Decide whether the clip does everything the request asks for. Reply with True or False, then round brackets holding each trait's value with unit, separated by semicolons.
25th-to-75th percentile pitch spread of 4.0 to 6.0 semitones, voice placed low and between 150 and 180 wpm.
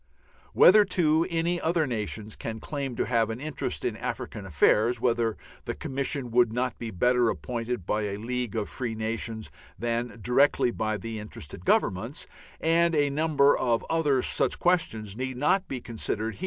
True (4.4 semitones; 120 Hz; 170 wpm)